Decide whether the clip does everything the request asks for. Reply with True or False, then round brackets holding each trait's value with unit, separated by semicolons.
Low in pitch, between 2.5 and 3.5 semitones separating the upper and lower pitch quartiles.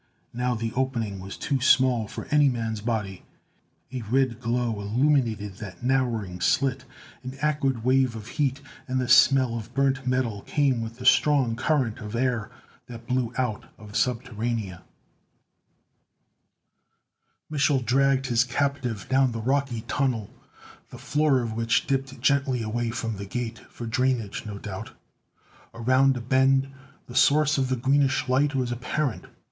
True (125 Hz; 2.9 semitones)